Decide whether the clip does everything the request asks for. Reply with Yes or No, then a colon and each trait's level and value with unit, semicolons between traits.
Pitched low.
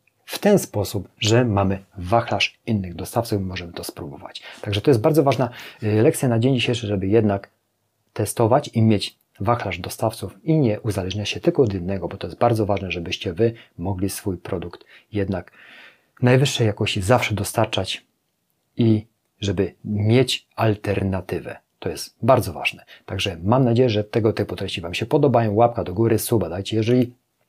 Yes: low, 110 Hz